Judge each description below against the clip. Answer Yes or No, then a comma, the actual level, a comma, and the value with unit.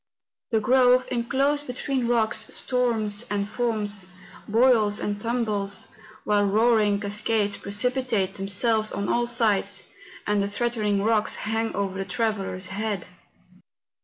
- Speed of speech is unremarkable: No, slow, 125 wpm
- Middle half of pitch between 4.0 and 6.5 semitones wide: No, average, 2.8 semitones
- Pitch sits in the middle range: No, high, 215 Hz